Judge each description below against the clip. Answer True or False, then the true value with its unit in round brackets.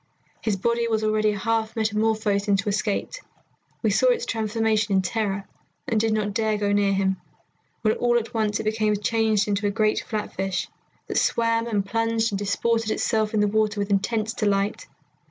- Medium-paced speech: True (185 wpm)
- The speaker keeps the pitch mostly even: True (1.7 semitones)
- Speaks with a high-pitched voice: True (215 Hz)